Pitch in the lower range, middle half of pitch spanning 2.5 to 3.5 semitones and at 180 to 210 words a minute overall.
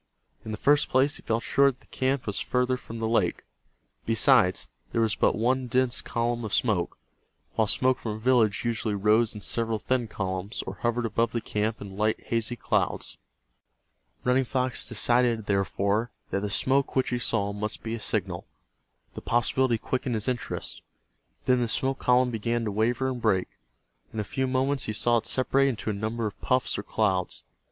Yes: low, 115 Hz; average, 3.0 semitones; average, 190 wpm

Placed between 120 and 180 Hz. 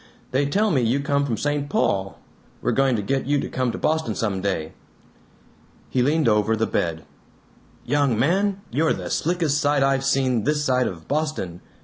Yes: low, 135 Hz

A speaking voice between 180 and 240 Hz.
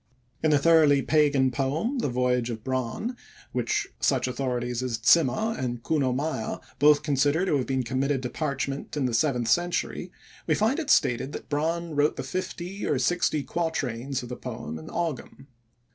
No: medium, 140 Hz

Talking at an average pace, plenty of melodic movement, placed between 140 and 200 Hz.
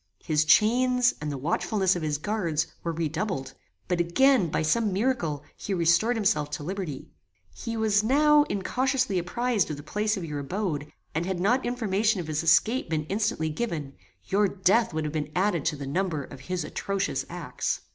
Yes: average, 180 wpm; wide, 5.8 semitones; medium, 185 Hz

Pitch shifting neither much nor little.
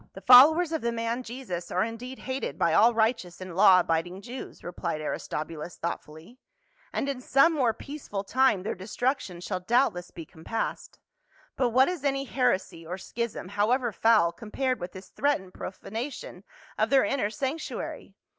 No: wide, 6.2 semitones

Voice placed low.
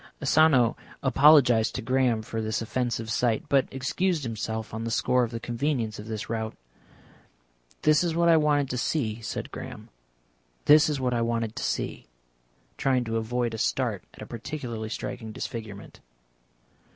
Yes: low, 120 Hz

